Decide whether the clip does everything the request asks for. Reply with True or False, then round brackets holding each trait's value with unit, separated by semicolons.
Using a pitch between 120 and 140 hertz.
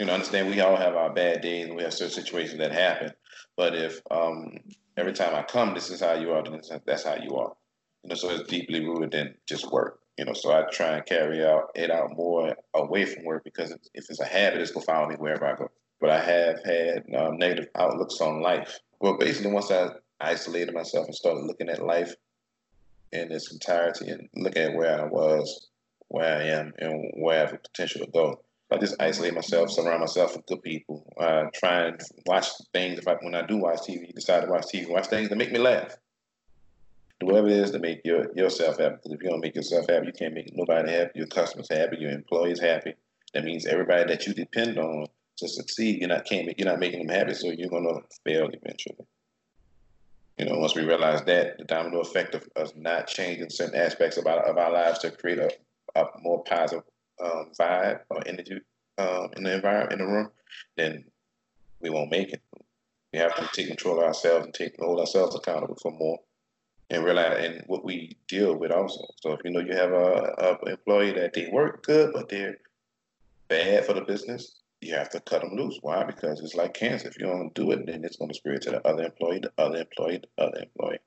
False (85 Hz)